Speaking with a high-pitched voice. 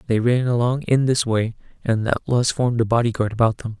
No: low, 115 Hz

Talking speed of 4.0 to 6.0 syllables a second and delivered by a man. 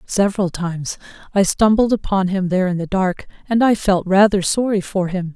No: 5.3 syllables/s; female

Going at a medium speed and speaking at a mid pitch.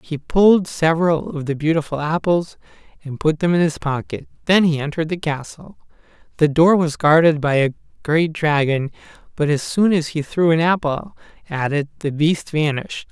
Yes: average, 180 wpm; medium, 155 Hz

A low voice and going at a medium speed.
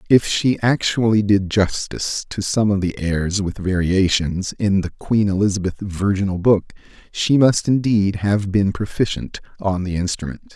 Yes: low, 100 Hz; average, 155 wpm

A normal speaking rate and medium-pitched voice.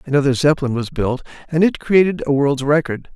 Yes: average, 190 wpm; medium, 145 Hz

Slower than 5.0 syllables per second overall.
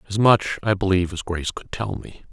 No: 6.0 syllables/s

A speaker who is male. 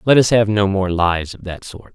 Yes: male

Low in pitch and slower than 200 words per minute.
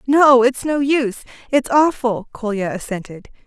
No: high, 245 Hz; average, 140 wpm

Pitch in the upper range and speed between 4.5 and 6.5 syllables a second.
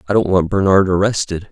No: very low, 95 Hz; 6.0 syllables/s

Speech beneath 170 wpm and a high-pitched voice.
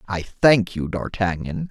No: average, 140 wpm; low, 100 Hz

